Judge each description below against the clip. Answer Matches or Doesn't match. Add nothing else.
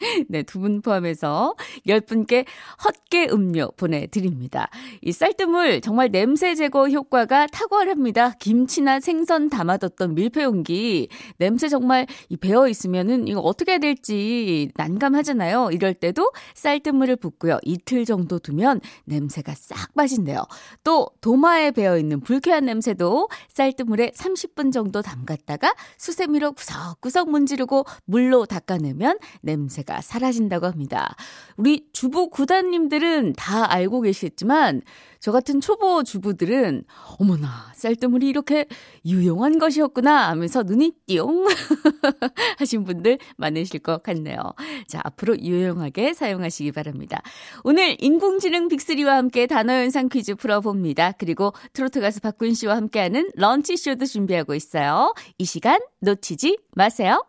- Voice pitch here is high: Matches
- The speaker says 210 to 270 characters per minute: Doesn't match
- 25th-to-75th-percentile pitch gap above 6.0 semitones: Matches